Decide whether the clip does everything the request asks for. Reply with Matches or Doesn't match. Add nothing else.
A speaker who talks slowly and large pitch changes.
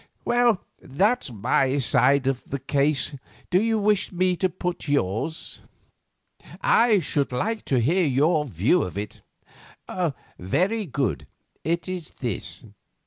Matches